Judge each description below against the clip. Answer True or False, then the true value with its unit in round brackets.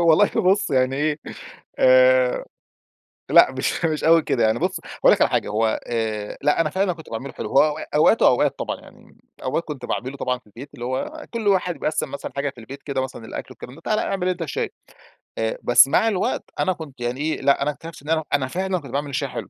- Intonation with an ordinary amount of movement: False (5.7 semitones)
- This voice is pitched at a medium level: True (150 Hz)